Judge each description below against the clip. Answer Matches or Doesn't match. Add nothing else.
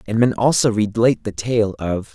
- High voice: Doesn't match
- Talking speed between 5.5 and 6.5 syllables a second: Doesn't match